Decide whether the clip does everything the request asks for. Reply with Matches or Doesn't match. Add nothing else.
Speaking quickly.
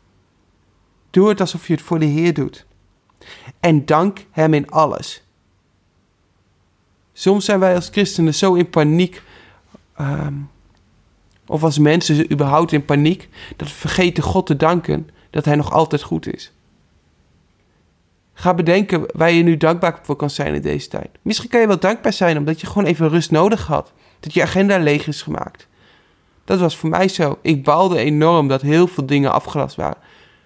Doesn't match